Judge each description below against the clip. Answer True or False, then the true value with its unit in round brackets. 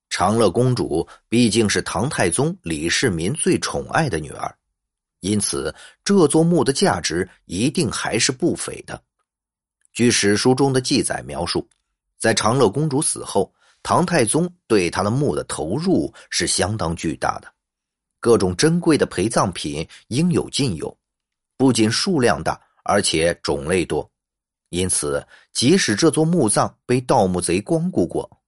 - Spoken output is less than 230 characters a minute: True (215 characters per minute)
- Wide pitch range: True (7.8 semitones)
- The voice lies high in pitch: False (125 Hz)